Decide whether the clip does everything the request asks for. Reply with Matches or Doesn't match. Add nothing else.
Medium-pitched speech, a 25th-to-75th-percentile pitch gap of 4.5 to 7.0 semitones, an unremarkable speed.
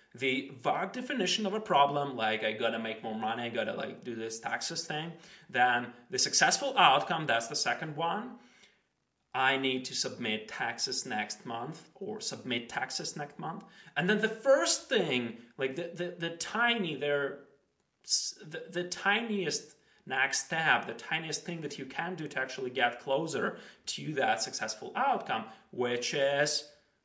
Matches